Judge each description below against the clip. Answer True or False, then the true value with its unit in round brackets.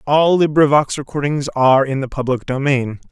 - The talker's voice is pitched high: False (140 Hz)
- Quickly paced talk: False (155 wpm)